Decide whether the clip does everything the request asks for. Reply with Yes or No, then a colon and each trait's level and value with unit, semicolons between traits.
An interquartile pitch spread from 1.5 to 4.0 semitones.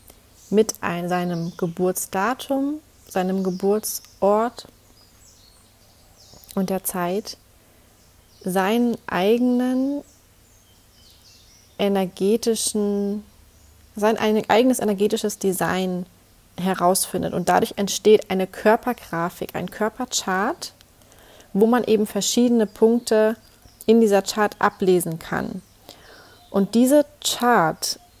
No: average, 4.6 semitones